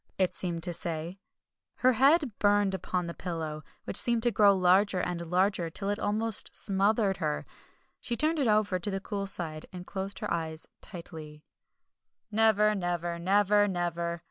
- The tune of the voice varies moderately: Yes, average, 3.4 semitones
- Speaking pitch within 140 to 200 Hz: Yes, high, 190 Hz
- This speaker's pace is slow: No, average, 165 wpm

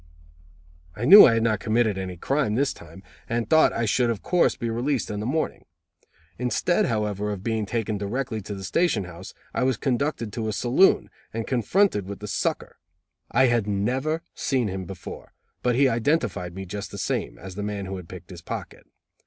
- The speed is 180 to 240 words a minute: Yes, average, 195 wpm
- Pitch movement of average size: Yes, average, 4.2 semitones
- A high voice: No, low, 110 Hz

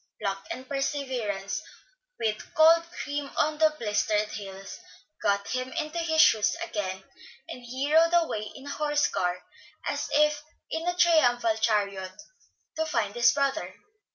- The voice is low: No, very high, 255 Hz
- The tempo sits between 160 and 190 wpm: No, average, 140 wpm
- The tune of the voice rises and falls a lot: Yes, wide, 6.9 semitones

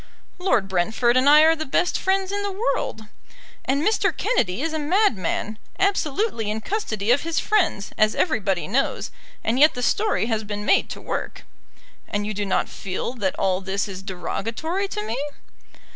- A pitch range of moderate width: No, wide, 8.6 semitones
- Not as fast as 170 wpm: No, average, 175 wpm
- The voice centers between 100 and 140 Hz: No, high, 240 Hz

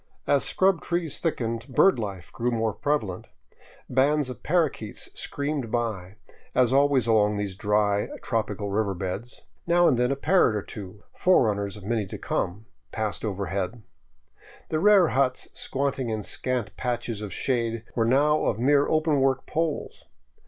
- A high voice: No, low, 120 Hz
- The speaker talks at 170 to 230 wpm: No, average, 155 wpm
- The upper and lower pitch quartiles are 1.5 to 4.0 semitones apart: No, average, 5.3 semitones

